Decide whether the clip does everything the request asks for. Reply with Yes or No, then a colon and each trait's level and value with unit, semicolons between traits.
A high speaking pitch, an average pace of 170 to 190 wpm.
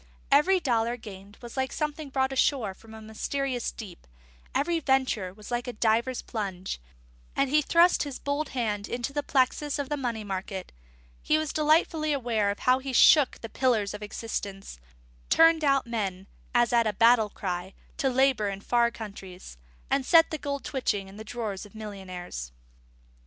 Yes: high, 240 Hz; average, 180 wpm